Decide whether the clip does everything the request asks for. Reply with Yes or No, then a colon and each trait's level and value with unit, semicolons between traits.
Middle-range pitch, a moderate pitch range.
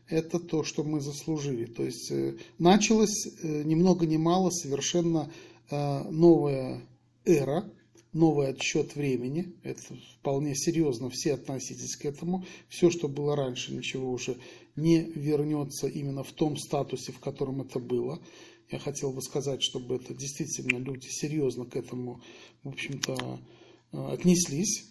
Yes: medium, 145 Hz; average, 3.8 semitones